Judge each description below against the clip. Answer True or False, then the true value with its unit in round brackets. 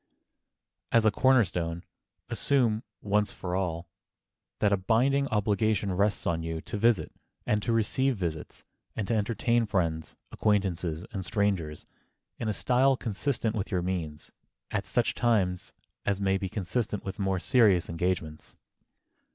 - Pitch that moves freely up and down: False (3.9 semitones)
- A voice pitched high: False (100 Hz)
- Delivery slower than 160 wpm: True (145 wpm)